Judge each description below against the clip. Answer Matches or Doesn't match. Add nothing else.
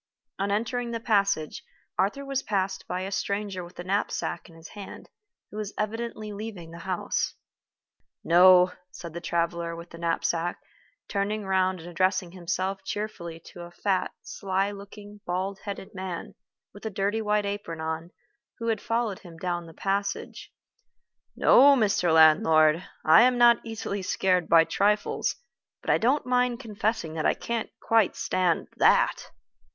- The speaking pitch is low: Doesn't match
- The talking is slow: Doesn't match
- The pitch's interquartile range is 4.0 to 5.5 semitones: Doesn't match